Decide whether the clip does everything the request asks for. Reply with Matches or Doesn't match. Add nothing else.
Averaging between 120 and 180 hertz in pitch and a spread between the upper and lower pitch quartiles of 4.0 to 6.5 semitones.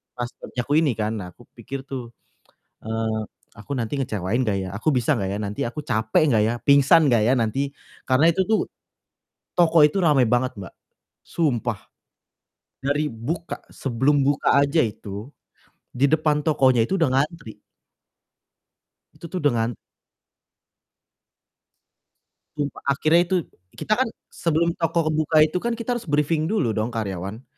Matches